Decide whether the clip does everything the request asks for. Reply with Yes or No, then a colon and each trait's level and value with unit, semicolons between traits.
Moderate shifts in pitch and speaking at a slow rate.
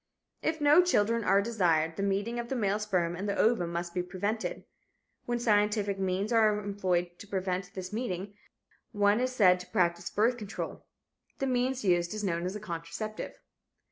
No: average, 3.7 semitones; average, 175 wpm